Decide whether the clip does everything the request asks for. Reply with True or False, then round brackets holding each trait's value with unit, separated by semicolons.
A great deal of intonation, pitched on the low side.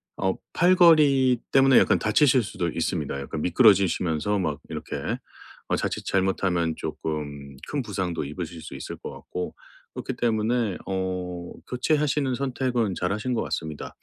True (6.9 semitones; 95 Hz)